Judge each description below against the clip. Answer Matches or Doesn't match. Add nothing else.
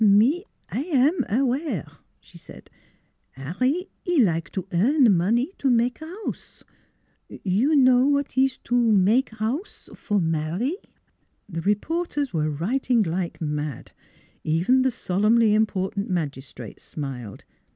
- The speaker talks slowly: Matches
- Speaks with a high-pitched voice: Matches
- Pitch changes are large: Matches